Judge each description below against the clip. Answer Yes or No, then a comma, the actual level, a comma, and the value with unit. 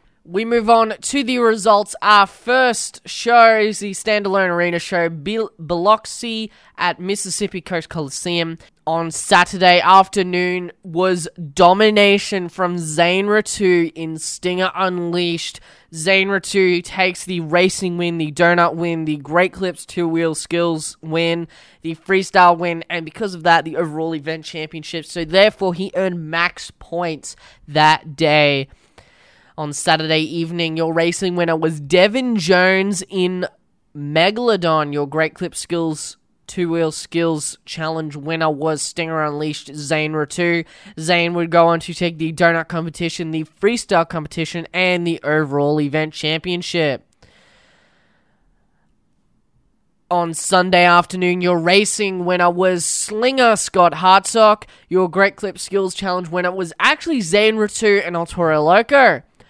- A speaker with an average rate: No, slow, 130 wpm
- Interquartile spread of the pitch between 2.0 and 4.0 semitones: Yes, average, 2.8 semitones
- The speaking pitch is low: No, medium, 175 Hz